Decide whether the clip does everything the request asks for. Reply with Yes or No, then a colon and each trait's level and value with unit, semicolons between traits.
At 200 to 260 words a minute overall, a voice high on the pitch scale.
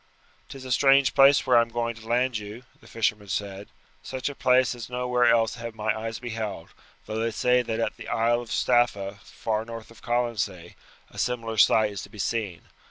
No: fast, 205 wpm; low, 115 Hz